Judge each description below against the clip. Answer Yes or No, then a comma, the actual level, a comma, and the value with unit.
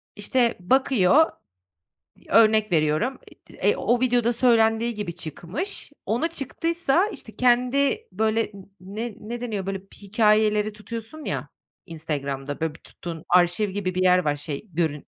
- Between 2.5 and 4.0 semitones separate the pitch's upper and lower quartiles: No, wide, 5.5 semitones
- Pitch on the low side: No, high, 215 Hz